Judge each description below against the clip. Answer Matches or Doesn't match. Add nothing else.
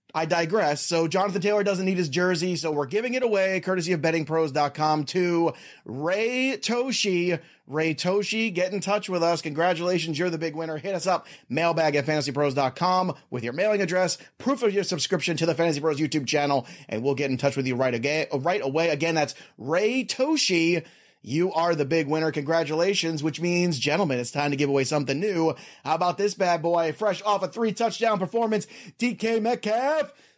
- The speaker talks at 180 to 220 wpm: Matches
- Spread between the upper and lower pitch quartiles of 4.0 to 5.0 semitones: Matches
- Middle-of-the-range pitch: Matches